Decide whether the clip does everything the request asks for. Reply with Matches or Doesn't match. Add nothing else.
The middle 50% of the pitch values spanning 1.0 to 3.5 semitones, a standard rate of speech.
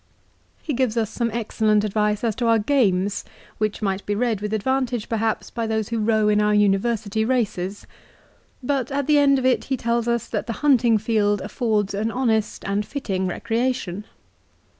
Matches